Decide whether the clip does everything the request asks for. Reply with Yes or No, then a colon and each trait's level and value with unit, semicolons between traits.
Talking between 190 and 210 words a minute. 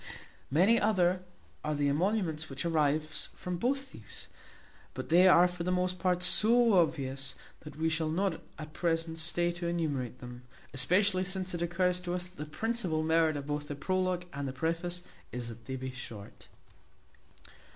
No: average, 170 wpm